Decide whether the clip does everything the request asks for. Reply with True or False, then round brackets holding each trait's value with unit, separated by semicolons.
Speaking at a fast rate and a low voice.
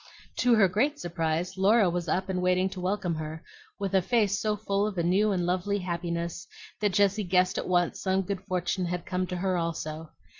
False (210 wpm; 185 Hz)